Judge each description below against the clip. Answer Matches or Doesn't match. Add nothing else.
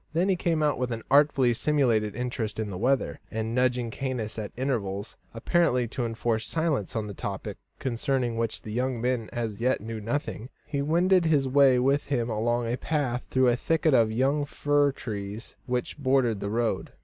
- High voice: Doesn't match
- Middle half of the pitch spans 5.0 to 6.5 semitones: Doesn't match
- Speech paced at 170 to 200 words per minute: Matches